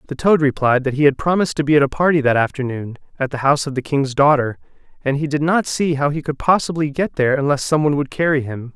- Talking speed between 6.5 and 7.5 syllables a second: Yes, 6.6 syllables/s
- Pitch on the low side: No, medium, 145 Hz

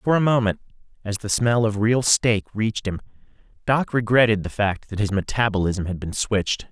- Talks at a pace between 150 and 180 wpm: No, average, 190 wpm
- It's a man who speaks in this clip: Yes, male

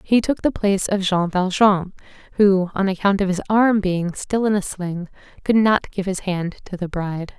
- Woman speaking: Yes, female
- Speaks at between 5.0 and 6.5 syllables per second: No, 4.8 syllables/s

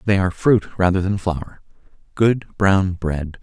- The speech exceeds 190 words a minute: No, average, 140 wpm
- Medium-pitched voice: No, very low, 95 Hz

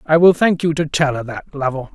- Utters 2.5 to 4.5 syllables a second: No, 5.4 syllables/s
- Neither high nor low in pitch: Yes, medium, 150 Hz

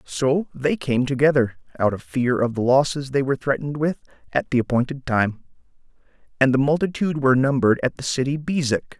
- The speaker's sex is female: No, male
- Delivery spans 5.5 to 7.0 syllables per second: Yes, 6.0 syllables/s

